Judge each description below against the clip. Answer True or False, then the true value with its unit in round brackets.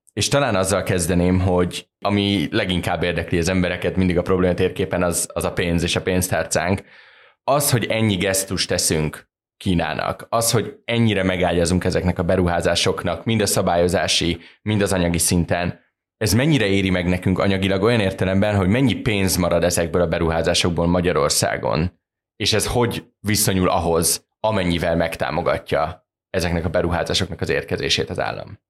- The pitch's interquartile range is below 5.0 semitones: True (2.9 semitones)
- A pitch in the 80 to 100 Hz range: True (95 Hz)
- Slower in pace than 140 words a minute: False (150 wpm)